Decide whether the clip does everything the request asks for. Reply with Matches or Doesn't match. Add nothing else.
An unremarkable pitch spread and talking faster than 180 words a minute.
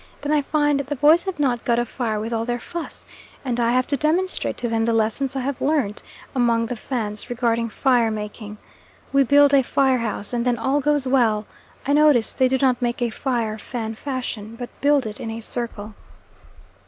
Matches